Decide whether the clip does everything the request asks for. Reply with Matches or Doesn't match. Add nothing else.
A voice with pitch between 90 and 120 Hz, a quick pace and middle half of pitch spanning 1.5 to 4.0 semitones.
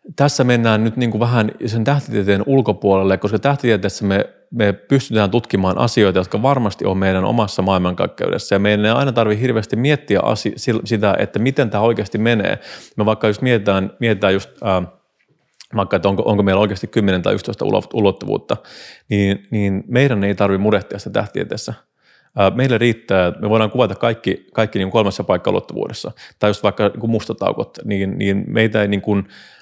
Matches